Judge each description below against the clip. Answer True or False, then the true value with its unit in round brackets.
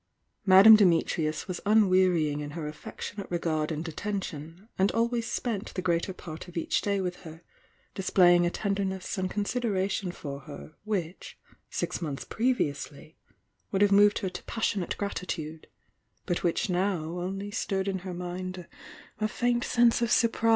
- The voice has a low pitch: False (185 Hz)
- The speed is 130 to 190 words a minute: True (160 wpm)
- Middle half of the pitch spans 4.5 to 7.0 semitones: False (3.5 semitones)